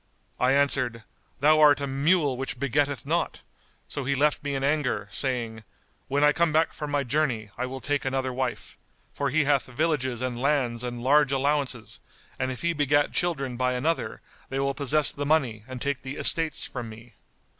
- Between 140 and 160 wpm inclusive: No, average, 190 wpm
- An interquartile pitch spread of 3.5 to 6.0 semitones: No, narrow, 2.6 semitones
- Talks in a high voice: No, low, 135 Hz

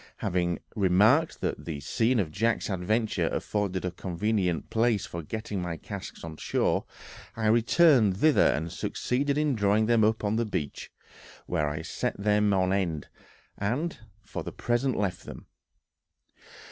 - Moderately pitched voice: No, low, 105 Hz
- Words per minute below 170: Yes, average, 150 wpm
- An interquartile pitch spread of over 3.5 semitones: Yes, average, 4.5 semitones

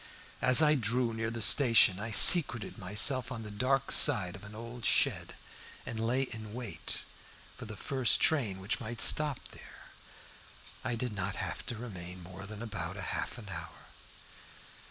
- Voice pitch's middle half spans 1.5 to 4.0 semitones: Yes, average, 3.7 semitones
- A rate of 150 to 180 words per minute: Yes, average, 165 wpm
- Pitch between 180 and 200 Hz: No, low, 115 Hz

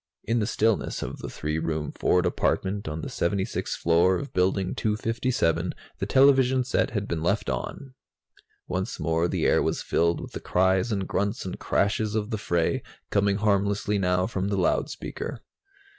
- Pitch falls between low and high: No, low, 100 Hz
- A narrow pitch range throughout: No, average, 3.4 semitones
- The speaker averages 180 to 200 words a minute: No, average, 170 wpm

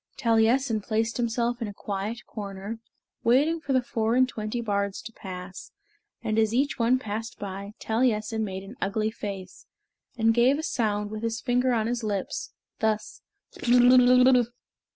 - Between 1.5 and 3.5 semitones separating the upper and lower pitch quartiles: Yes, average, 2.7 semitones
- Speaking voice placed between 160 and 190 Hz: No, high, 225 Hz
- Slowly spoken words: No, average, 160 wpm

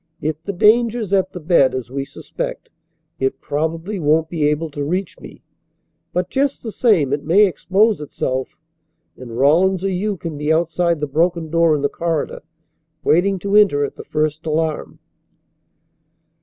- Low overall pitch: No, medium, 165 Hz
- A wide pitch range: No, average, 4.2 semitones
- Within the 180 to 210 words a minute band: No, average, 165 wpm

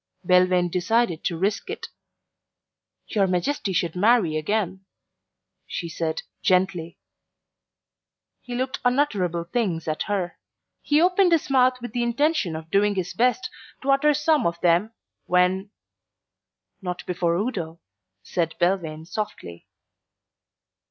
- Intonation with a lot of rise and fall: Yes, wide, 6.2 semitones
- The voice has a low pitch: No, high, 190 Hz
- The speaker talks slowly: Yes, slow, 120 wpm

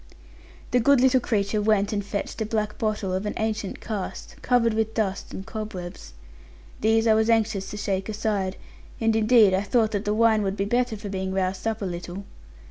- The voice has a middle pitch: No, high, 215 Hz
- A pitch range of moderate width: No, narrow, 2.2 semitones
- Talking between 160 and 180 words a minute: No, average, 200 wpm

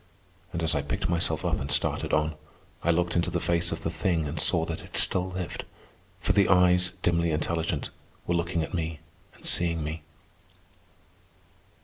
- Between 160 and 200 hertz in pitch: No, very low, 85 Hz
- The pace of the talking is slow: No, average, 175 wpm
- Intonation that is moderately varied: No, narrow, 1.5 semitones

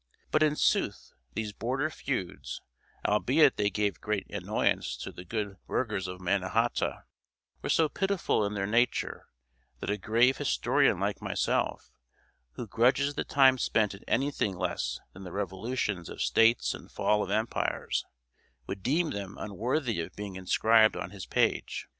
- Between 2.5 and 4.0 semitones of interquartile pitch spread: No, average, 4.6 semitones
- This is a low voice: Yes, low, 105 Hz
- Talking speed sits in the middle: Yes, average, 155 wpm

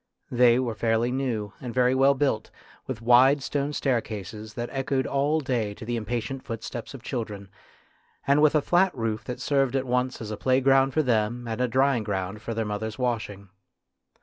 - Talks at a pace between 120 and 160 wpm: No, average, 185 wpm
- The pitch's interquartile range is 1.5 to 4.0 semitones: Yes, average, 3.4 semitones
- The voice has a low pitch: Yes, low, 120 Hz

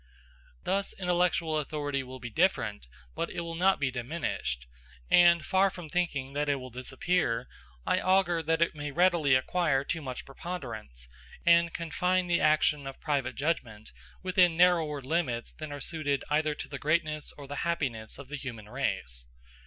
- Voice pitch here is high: No, medium, 150 Hz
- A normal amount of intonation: Yes, average, 4.5 semitones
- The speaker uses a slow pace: No, average, 165 wpm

